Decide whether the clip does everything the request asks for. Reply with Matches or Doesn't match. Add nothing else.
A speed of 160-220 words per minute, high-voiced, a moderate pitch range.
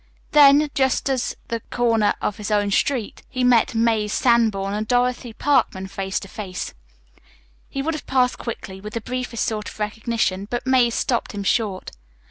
Matches